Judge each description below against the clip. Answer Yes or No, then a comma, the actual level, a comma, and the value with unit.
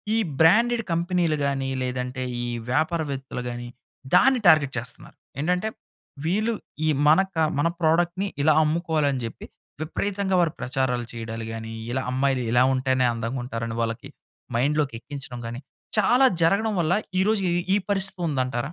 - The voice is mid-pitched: Yes, medium, 145 Hz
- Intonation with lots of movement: Yes, wide, 5.8 semitones